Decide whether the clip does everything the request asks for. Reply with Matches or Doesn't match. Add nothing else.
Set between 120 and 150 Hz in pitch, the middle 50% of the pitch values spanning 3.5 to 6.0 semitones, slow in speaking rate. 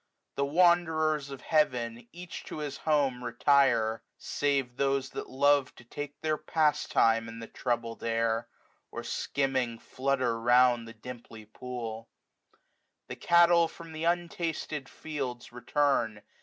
Matches